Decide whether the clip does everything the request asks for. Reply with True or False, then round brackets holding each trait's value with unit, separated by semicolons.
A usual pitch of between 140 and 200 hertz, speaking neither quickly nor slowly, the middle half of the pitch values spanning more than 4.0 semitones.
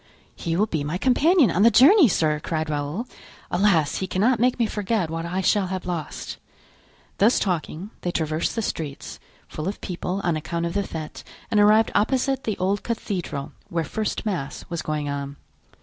True (185 Hz; 180 wpm; 5.1 semitones)